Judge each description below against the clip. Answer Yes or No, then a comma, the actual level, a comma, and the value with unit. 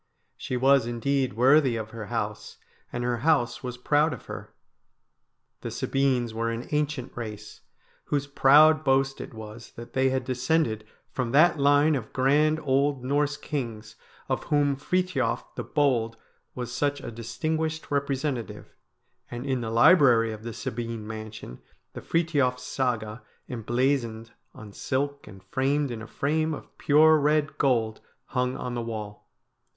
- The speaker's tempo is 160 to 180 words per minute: No, average, 150 wpm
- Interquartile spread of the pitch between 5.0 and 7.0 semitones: No, average, 3.9 semitones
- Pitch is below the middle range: Yes, low, 130 Hz